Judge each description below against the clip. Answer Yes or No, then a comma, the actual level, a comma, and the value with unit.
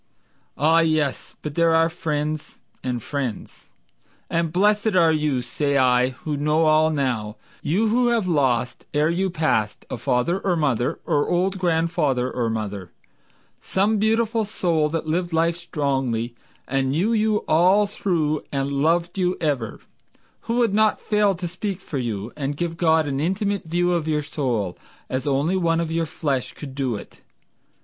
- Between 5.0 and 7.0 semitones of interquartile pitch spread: No, average, 4.6 semitones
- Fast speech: No, average, 165 wpm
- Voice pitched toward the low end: No, medium, 160 Hz